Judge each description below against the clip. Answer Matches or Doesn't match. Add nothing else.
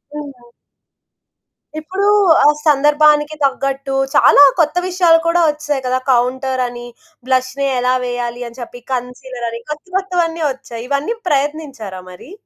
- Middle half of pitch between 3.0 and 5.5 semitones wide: Matches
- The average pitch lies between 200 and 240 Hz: Doesn't match